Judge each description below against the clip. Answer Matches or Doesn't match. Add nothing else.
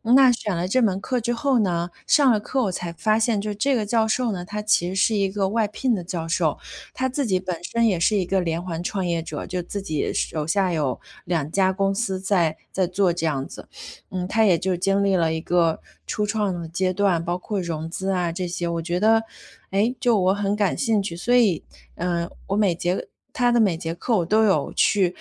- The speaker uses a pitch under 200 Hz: Matches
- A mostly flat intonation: Doesn't match